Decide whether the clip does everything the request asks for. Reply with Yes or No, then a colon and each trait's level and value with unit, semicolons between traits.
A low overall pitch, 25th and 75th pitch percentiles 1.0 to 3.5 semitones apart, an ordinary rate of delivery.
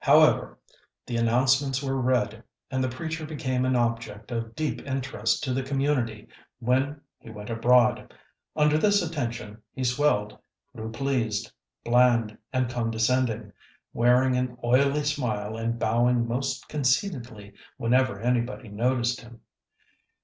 No: low, 125 Hz; narrow, 2.5 semitones; slow, 125 wpm